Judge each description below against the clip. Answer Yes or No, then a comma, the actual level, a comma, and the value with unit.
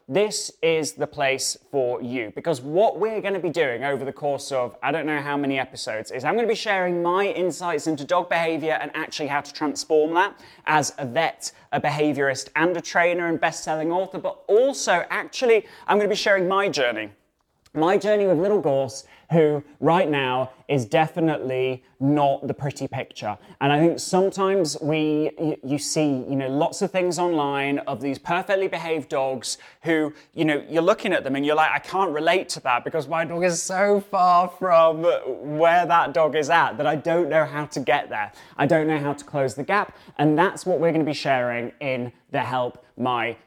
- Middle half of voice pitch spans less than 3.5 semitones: No, average, 3.9 semitones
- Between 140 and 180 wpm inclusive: No, fast, 205 wpm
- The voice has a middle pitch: Yes, medium, 155 Hz